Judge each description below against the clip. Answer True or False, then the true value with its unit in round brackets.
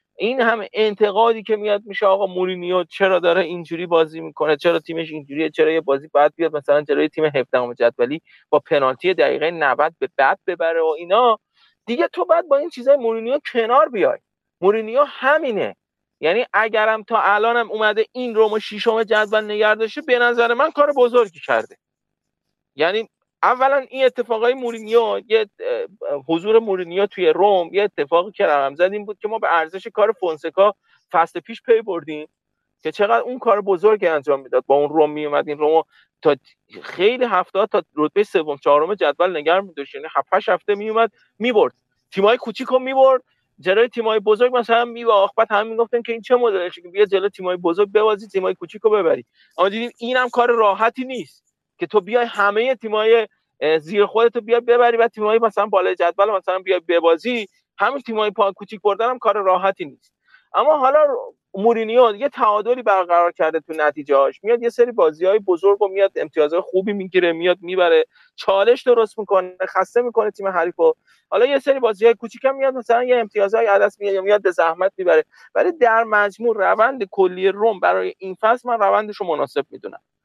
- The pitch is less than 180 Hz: False (215 Hz)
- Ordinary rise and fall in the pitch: True (4.8 semitones)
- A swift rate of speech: True (175 wpm)